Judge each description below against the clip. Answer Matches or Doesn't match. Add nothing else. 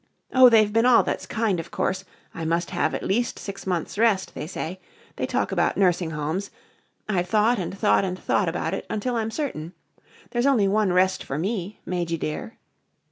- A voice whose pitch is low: Doesn't match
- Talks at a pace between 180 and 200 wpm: Matches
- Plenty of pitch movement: Doesn't match